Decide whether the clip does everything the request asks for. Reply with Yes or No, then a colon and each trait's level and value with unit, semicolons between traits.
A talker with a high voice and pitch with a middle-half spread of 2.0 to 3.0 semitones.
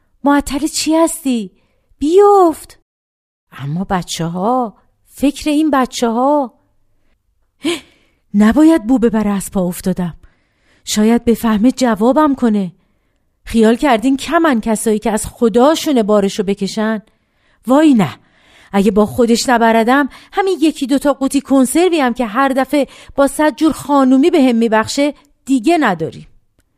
No: very high, 250 Hz; average, 5.2 semitones